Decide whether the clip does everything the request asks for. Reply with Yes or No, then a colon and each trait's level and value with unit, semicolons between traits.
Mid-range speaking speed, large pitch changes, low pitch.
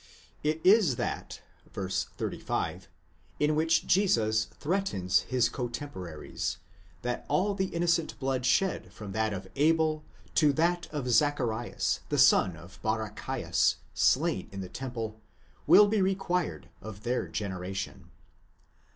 No: slow, 125 wpm; wide, 7.6 semitones; low, 125 Hz